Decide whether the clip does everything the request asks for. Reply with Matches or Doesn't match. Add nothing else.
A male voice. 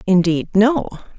Doesn't match